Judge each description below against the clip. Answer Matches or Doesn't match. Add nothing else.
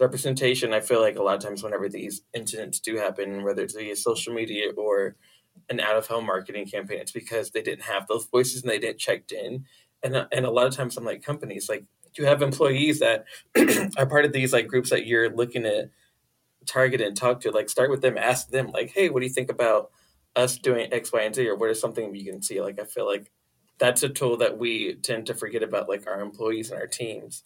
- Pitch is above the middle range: Doesn't match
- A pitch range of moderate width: Doesn't match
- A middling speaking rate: Doesn't match